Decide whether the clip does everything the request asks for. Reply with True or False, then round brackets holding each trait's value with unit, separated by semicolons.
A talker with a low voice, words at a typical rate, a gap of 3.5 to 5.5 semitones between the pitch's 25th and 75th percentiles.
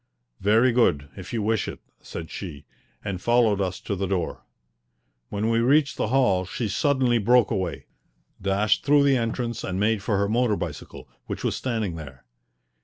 True (105 Hz; 175 wpm; 4.2 semitones)